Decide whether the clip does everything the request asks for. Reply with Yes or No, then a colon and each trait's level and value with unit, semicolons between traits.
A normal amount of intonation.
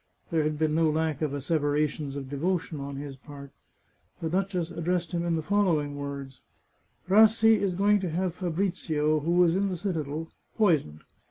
Yes: average, 3.8 semitones